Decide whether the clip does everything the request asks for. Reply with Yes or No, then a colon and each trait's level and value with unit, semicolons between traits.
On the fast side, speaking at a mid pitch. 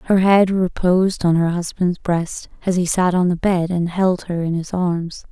Yes: fast, 215 wpm; medium, 180 Hz